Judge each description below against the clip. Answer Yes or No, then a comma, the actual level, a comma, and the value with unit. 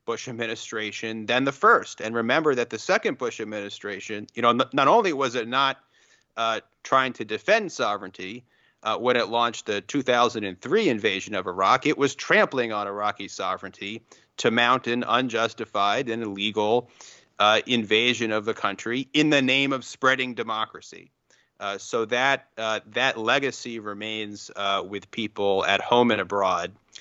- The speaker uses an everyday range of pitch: Yes, average, 3.1 semitones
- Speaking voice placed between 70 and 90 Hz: No, low, 115 Hz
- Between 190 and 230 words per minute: No, average, 155 wpm